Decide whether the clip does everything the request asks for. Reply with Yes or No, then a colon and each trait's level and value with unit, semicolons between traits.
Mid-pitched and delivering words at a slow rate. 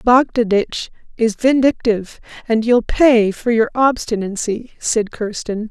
No: high, 230 Hz; slow, 115 wpm